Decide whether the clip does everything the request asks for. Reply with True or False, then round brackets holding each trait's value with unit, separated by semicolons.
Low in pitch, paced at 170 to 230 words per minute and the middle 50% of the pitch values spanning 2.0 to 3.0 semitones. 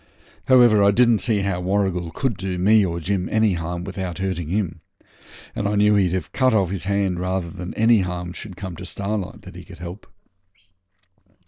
True (95 Hz; 195 wpm; 2.7 semitones)